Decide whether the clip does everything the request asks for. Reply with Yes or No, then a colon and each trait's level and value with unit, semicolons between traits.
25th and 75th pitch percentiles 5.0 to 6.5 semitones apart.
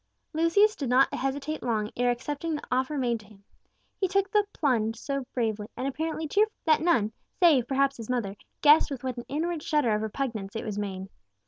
Yes: wide, 5.5 semitones